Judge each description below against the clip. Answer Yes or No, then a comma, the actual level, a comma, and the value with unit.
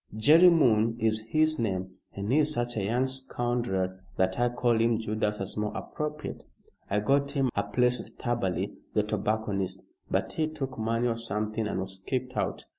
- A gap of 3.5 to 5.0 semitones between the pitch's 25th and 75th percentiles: Yes, average, 3.9 semitones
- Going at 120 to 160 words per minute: No, average, 180 wpm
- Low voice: Yes, low, 115 Hz